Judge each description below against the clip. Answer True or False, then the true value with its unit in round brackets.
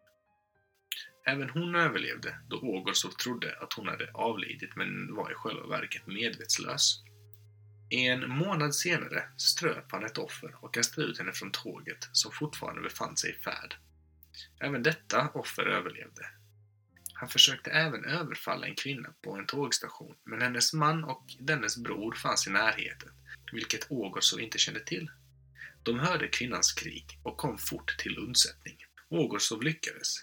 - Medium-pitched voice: False (125 Hz)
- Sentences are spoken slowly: False (145 wpm)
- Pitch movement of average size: False (7.1 semitones)